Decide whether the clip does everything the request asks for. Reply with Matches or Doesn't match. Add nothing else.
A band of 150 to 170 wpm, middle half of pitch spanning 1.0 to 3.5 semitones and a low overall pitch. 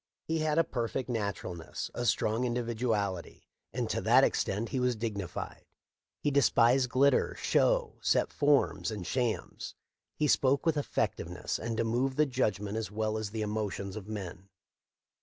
Doesn't match